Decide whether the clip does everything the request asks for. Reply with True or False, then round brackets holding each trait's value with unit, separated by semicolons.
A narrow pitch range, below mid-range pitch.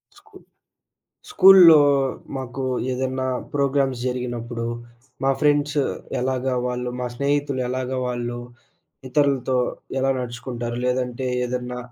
True (1.9 semitones; 130 Hz)